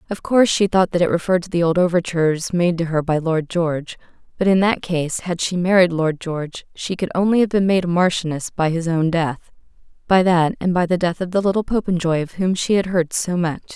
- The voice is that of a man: No, female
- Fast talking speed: Yes, fast, 235 wpm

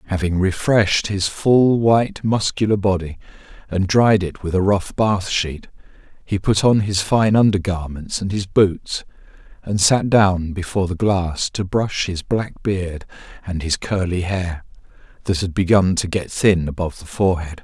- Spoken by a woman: No, male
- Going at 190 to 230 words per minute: No, average, 165 wpm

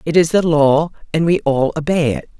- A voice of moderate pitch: Yes, medium, 155 Hz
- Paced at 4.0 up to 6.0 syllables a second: Yes, 5.2 syllables/s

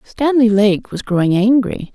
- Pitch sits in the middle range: No, high, 220 Hz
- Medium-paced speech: Yes, average, 155 wpm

